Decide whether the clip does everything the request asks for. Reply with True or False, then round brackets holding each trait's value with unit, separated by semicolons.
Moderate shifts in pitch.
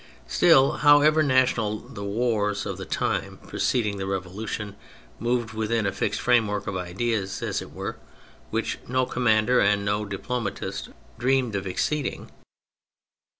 True (3.7 semitones)